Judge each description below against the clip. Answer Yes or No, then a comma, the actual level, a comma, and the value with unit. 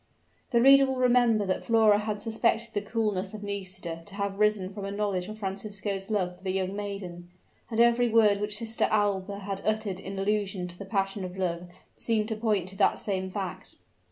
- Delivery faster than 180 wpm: Yes, average, 200 wpm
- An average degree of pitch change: No, narrow, 2.2 semitones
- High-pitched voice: Yes, high, 205 Hz